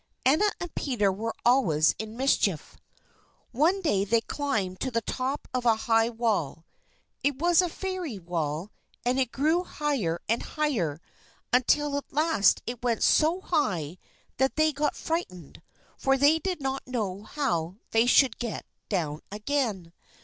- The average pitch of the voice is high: Yes, high, 245 Hz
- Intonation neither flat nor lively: No, wide, 6.9 semitones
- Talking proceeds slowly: No, average, 150 wpm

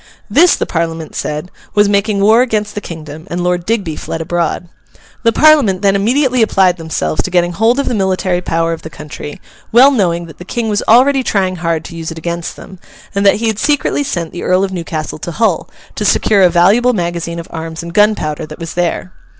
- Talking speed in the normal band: No, fast, 215 wpm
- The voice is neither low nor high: Yes, medium, 180 Hz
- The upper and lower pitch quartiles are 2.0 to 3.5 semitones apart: No, average, 4.4 semitones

